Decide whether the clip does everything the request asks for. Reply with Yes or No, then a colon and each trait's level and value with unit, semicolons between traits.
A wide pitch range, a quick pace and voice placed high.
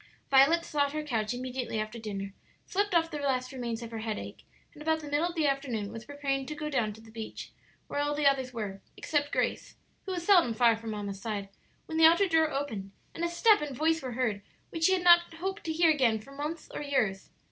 Yes: wide, 6.0 semitones; fast, 235 wpm; very high, 275 Hz